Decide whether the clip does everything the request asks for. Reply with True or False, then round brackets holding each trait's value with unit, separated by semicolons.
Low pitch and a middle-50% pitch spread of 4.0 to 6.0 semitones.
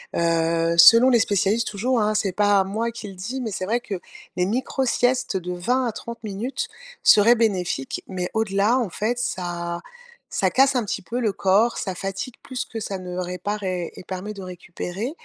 False (205 Hz; 4.3 semitones)